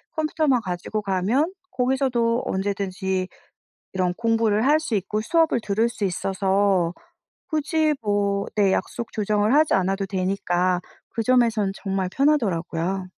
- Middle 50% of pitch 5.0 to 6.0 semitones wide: No, average, 4.3 semitones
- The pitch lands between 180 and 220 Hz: Yes, high, 205 Hz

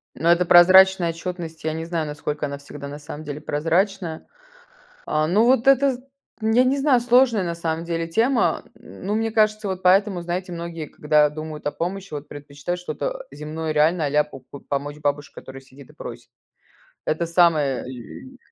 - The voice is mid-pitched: Yes, medium, 170 Hz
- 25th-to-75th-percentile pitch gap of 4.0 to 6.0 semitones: Yes, average, 4.6 semitones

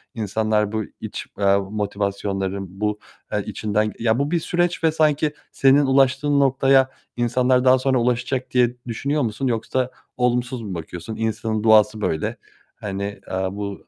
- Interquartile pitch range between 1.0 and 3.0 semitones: No, average, 4.3 semitones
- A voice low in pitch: Yes, low, 115 Hz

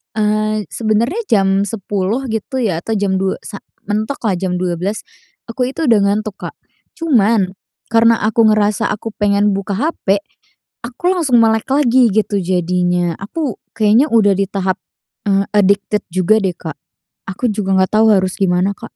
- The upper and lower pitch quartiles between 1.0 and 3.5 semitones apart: Yes, average, 2.8 semitones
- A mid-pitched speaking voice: No, high, 210 Hz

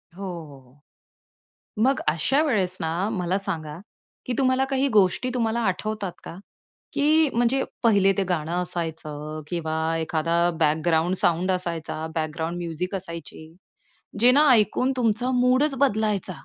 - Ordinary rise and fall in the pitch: No, wide, 6.6 semitones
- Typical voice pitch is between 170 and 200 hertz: Yes, medium, 180 Hz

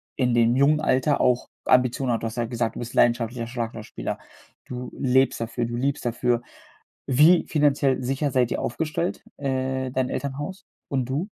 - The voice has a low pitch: Yes, low, 130 Hz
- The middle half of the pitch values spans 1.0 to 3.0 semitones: Yes, average, 2.7 semitones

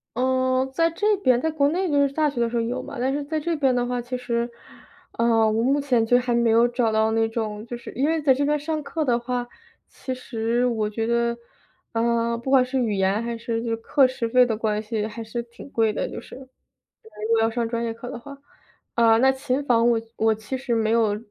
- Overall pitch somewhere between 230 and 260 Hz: Yes, high, 240 Hz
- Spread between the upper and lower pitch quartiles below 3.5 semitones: Yes, average, 2.7 semitones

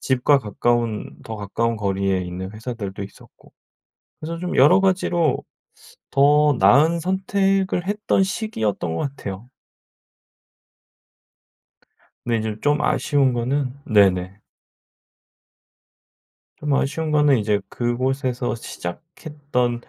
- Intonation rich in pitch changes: Yes, wide, 6.2 semitones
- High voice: No, low, 130 Hz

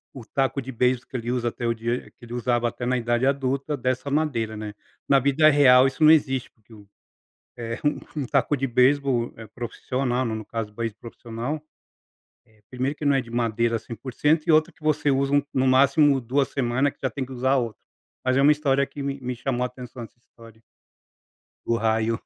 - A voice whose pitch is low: Yes, low, 125 Hz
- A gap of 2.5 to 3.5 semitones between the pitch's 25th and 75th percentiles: Yes, average, 2.8 semitones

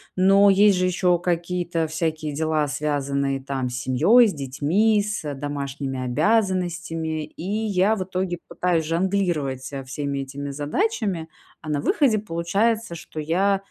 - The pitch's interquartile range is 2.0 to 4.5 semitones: No, average, 5.0 semitones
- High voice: No, medium, 165 Hz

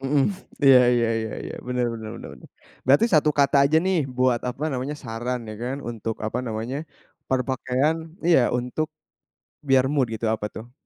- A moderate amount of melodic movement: Yes, average, 3.2 semitones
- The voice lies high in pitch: No, low, 125 Hz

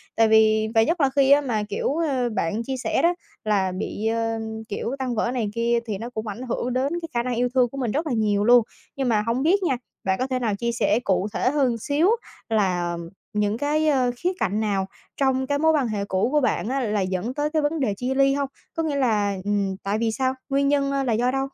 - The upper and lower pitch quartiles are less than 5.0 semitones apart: Yes, average, 4.3 semitones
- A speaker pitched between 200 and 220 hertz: No, high, 245 Hz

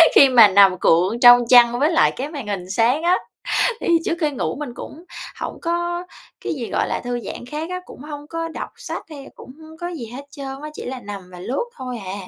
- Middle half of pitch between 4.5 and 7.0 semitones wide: Yes, average, 5.0 semitones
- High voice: Yes, very high, 270 Hz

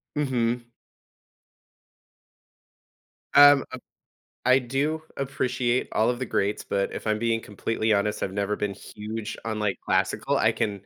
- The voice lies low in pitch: Yes, low, 115 Hz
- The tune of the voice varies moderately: Yes, average, 3.4 semitones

